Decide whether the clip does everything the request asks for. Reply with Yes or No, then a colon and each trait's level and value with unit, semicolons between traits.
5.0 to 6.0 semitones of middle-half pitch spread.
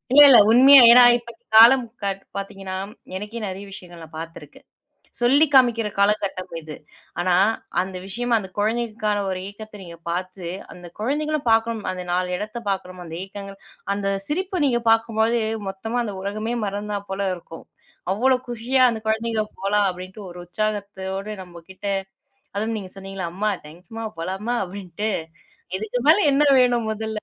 No: average, 3.6 semitones